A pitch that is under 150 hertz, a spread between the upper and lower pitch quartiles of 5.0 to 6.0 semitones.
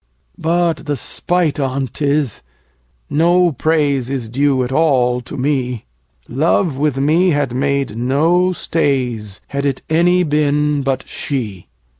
No: medium, 140 Hz; average, 3.5 semitones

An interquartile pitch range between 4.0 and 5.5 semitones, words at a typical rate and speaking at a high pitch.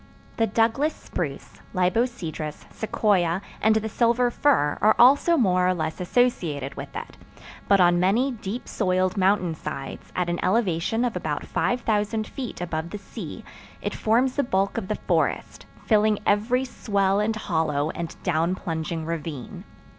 Yes: average, 5.0 semitones; average, 150 wpm; high, 195 Hz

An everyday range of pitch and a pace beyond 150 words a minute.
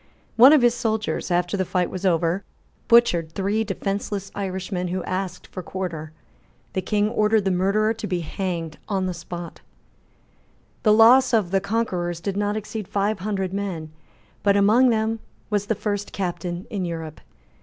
Yes: average, 3.1 semitones; average, 165 wpm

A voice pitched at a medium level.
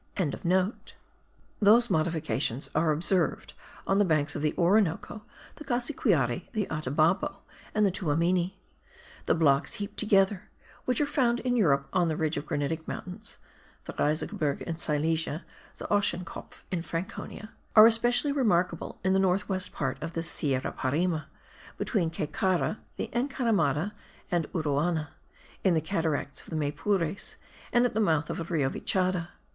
Yes: medium, 175 Hz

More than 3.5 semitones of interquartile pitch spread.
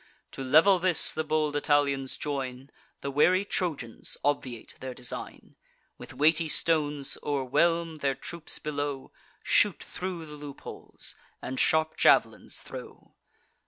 No: average, 2.7 semitones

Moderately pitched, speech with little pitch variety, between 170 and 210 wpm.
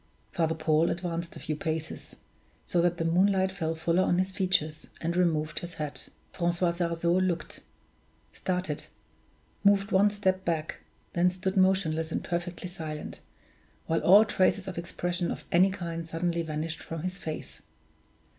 No: medium, 170 Hz; narrow, 2.3 semitones; average, 150 wpm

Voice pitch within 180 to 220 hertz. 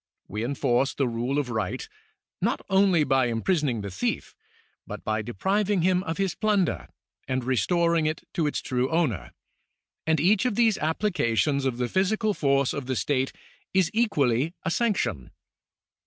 No: medium, 145 Hz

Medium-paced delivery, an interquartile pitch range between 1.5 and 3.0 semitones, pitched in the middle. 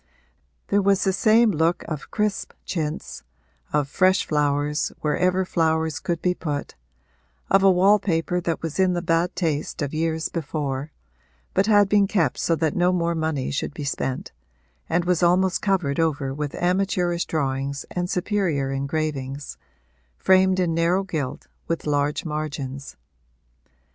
No: average, 150 wpm; average, 3.8 semitones; medium, 165 Hz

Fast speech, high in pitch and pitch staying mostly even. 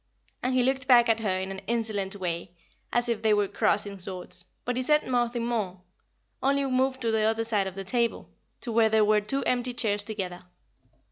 No: fast, 210 wpm; high, 225 Hz; average, 3.5 semitones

